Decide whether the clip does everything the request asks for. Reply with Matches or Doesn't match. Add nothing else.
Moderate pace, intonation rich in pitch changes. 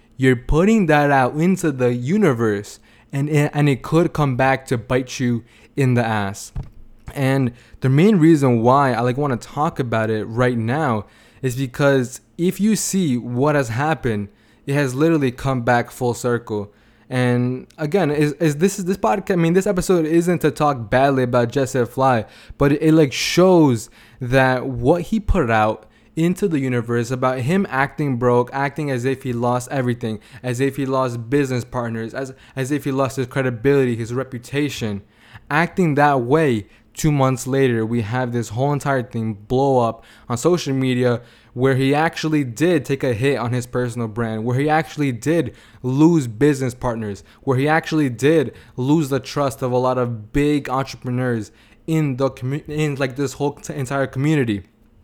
Doesn't match